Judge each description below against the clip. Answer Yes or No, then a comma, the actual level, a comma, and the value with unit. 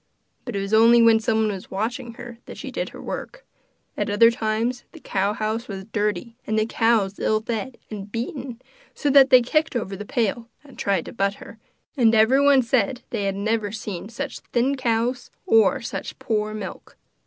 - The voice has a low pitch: No, high, 225 Hz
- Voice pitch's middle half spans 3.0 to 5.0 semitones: No, narrow, 2.6 semitones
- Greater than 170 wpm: Yes, average, 190 wpm